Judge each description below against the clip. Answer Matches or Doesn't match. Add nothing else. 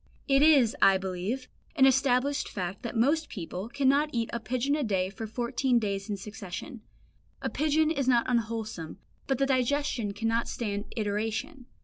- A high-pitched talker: Matches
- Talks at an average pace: Matches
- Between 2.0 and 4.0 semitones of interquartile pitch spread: Doesn't match